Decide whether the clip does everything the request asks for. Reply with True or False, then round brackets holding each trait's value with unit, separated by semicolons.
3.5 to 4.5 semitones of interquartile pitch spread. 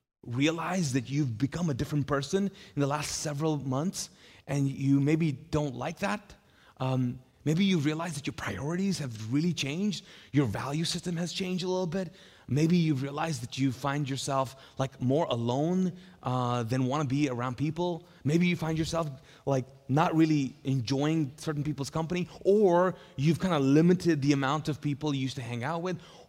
True (3.8 semitones)